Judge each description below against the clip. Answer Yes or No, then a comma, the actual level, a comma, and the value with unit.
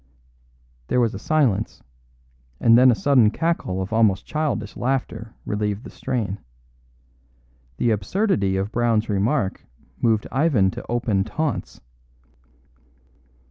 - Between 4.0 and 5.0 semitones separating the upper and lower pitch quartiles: Yes, average, 4.3 semitones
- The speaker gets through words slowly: Yes, slow, 115 wpm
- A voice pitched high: No, low, 115 Hz